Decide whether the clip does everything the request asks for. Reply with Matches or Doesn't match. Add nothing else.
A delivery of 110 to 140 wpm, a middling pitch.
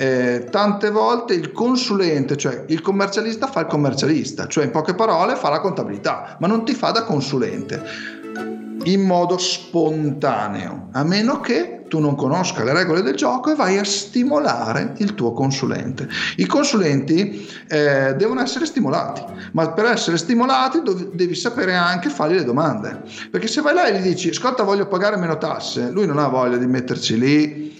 Doesn't match